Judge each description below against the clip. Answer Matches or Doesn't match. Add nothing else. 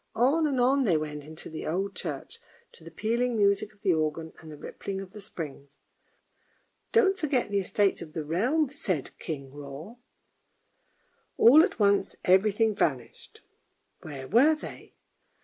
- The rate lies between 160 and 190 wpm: Matches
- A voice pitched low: Doesn't match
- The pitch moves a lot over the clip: Matches